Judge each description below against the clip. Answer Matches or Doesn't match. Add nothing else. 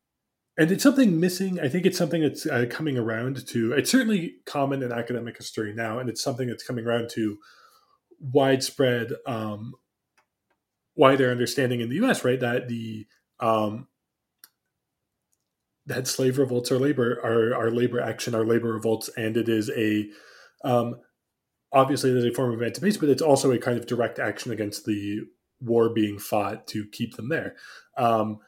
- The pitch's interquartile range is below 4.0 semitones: Matches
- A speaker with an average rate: Matches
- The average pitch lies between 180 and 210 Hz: Doesn't match